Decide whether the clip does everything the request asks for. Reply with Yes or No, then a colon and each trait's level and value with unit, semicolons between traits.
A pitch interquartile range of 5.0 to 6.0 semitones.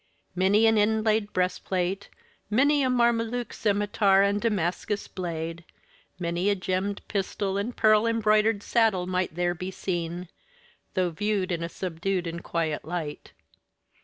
No: average, 3.3 semitones